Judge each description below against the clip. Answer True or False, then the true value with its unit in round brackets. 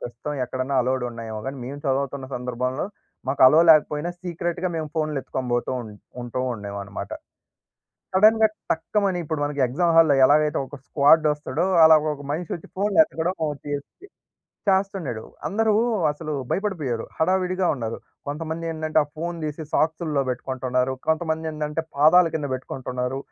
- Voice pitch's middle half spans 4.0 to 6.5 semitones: True (4.3 semitones)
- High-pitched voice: False (150 Hz)